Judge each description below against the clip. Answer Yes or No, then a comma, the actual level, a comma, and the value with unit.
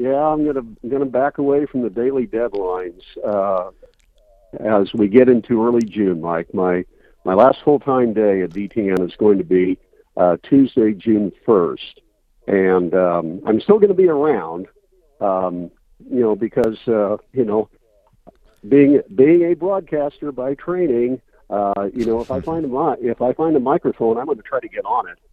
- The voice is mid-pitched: No, low, 120 Hz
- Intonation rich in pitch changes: Yes, wide, 6.8 semitones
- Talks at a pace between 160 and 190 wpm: Yes, average, 180 wpm